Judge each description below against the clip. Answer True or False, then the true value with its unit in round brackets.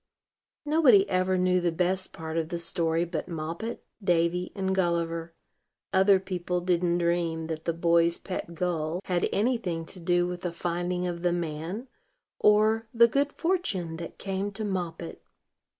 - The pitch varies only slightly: True (2.2 semitones)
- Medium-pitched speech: True (175 Hz)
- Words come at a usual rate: True (160 wpm)